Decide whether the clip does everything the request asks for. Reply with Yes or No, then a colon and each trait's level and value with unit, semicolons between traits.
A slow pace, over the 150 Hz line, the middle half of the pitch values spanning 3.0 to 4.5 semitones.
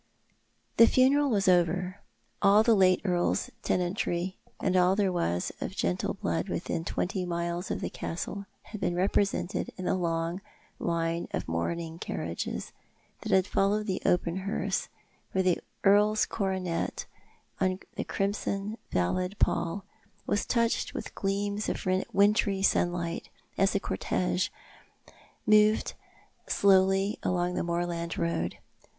No: slow, 130 wpm; medium, 185 Hz; narrow, 2.6 semitones